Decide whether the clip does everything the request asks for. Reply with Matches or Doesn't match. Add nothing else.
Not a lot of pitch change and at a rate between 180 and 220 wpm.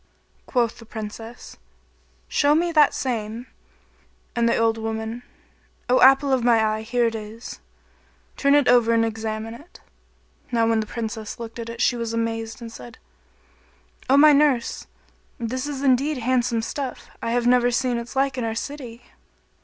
Doesn't match